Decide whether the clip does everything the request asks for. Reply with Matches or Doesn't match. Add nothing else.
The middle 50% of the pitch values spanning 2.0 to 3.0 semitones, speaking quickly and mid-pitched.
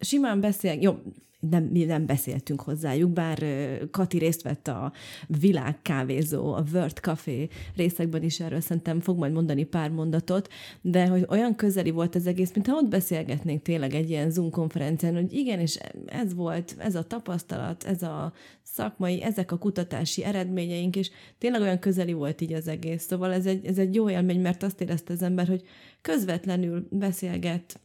Matches